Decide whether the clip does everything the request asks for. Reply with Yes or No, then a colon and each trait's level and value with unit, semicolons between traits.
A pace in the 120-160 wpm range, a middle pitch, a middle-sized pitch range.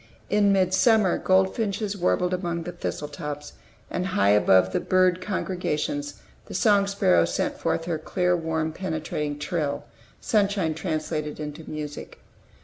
Yes: slow, 135 wpm; medium, 175 Hz; average, 4.0 semitones